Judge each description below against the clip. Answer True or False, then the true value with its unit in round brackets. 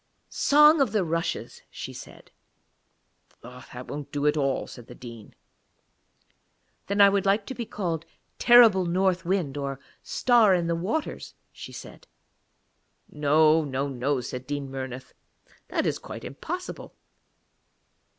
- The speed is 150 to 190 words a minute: False (135 wpm)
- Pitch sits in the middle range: True (165 Hz)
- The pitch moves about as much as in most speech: False (6.5 semitones)